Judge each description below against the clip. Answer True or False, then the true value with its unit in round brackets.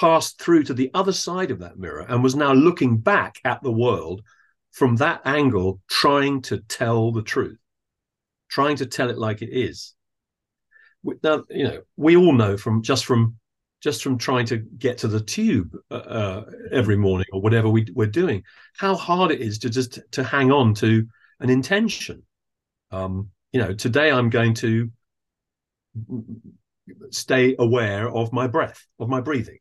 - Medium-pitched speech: False (125 Hz)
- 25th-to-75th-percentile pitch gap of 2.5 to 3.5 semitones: False (3.9 semitones)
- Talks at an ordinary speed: True (170 wpm)